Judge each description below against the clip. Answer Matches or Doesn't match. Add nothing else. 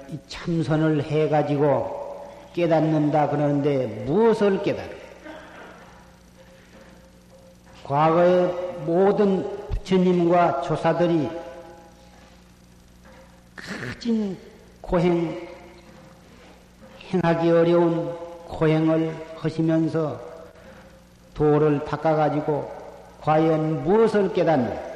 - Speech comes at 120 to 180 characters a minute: Matches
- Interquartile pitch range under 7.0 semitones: Matches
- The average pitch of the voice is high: Doesn't match